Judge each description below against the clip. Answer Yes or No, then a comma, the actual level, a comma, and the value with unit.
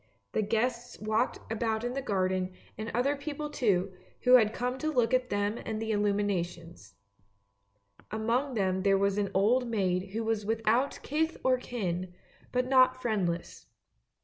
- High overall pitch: Yes, high, 220 Hz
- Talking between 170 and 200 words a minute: No, average, 160 wpm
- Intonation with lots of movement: No, average, 4.2 semitones